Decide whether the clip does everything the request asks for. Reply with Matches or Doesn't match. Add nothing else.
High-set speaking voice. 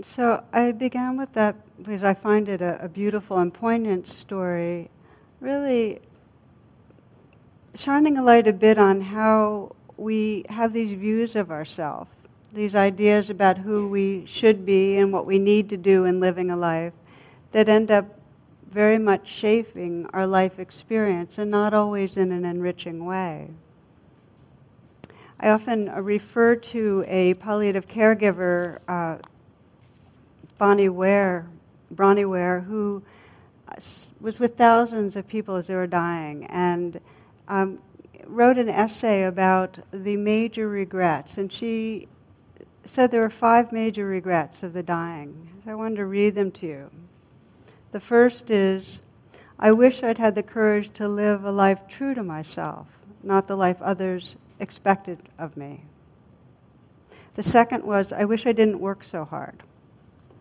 Matches